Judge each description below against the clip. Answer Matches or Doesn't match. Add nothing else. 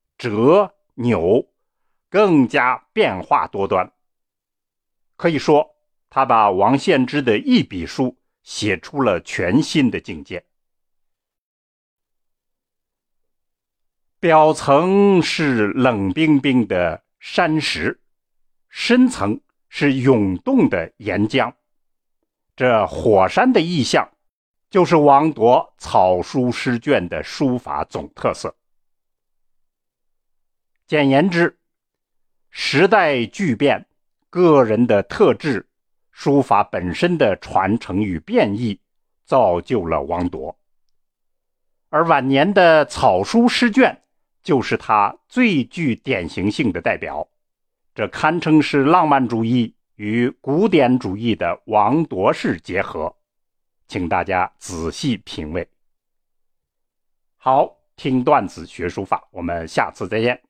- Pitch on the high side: Doesn't match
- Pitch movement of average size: Doesn't match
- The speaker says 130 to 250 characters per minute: Matches